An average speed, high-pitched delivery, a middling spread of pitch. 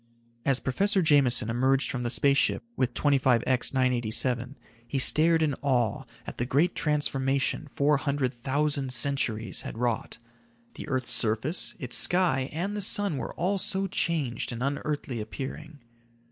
No: average, 145 wpm; low, 135 Hz; average, 3.4 semitones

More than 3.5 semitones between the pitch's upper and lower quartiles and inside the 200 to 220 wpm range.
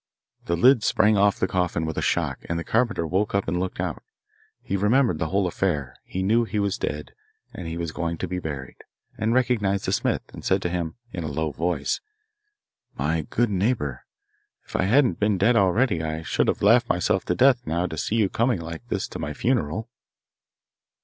Yes: average, 5.1 semitones; fast, 205 wpm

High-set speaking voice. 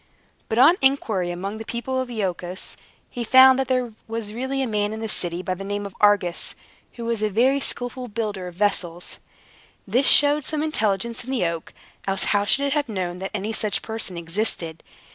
Yes: high, 215 Hz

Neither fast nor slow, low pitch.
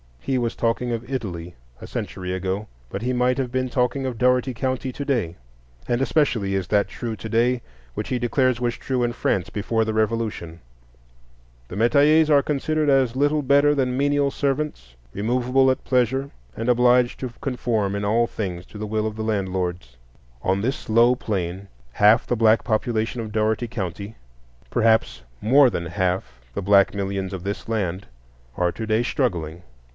Yes: average, 170 wpm; low, 115 Hz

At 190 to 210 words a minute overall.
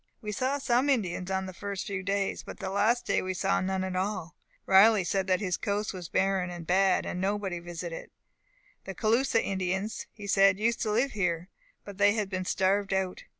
Yes: average, 200 wpm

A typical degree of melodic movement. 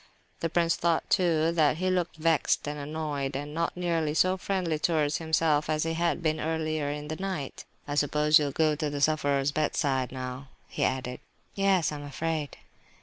No: narrow, 2.3 semitones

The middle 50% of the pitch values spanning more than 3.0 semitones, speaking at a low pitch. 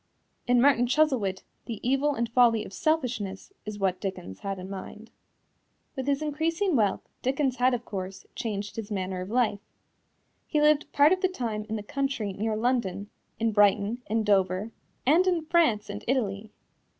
No: average, 5.2 semitones; high, 225 Hz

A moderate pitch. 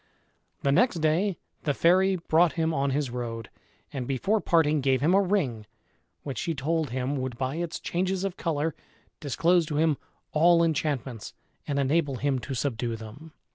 Yes: medium, 150 Hz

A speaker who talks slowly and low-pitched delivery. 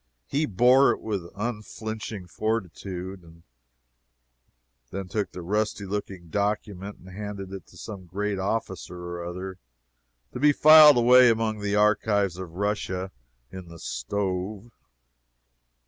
Yes: slow, 125 wpm; low, 100 Hz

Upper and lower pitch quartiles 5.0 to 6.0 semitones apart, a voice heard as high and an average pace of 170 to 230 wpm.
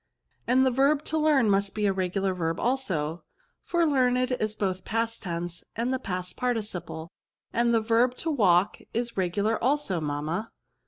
Yes: wide, 5.6 semitones; high, 220 Hz; average, 175 wpm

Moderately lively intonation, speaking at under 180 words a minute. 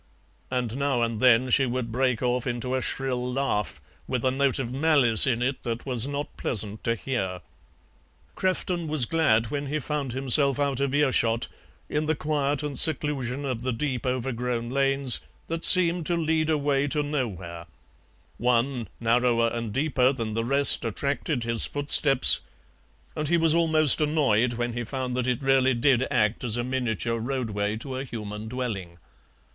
Yes: average, 3.3 semitones; average, 170 wpm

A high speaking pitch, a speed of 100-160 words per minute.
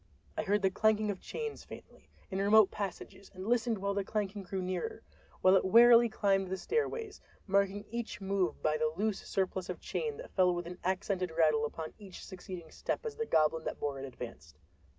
No: high, 195 Hz; average, 190 wpm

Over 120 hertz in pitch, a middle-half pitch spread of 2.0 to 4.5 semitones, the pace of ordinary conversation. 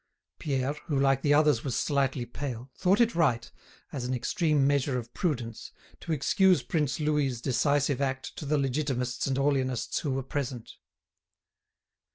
Yes: low, 135 Hz; average, 2.7 semitones; average, 155 wpm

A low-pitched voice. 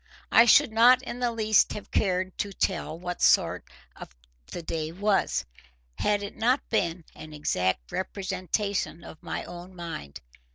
No: high, 190 Hz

